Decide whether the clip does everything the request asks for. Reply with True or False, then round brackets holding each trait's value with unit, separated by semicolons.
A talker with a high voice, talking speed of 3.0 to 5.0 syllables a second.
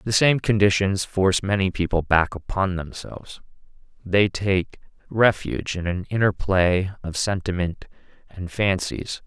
False (95 Hz; 4.4 syllables/s)